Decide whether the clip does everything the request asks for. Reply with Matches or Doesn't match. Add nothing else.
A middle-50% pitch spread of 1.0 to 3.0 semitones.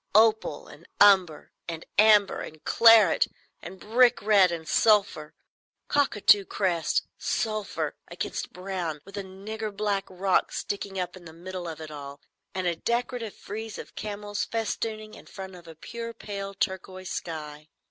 Doesn't match